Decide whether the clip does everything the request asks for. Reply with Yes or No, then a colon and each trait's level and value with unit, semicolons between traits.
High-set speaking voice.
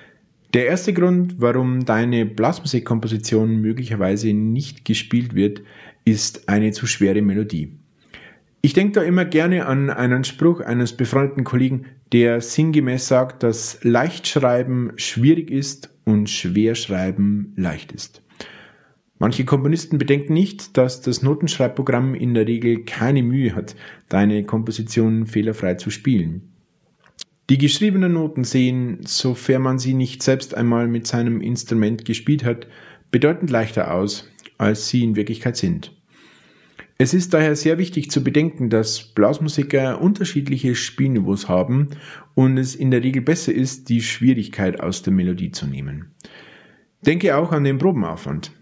No: low, 125 Hz